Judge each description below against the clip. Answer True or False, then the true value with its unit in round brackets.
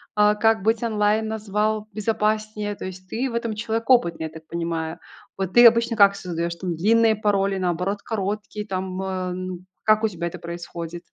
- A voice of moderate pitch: False (205 Hz)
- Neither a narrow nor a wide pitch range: True (3.3 semitones)